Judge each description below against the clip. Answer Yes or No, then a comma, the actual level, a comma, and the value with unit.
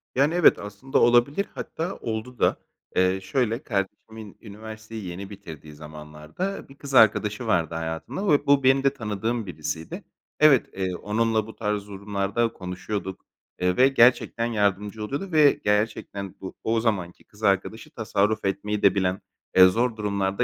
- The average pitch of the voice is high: No, low, 105 Hz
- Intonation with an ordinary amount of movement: Yes, average, 3.7 semitones